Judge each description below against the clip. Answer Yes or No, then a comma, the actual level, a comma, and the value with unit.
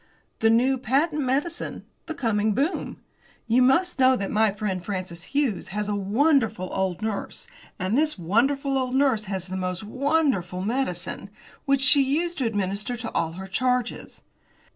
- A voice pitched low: No, high, 225 Hz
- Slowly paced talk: No, average, 160 wpm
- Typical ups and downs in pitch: No, wide, 5.8 semitones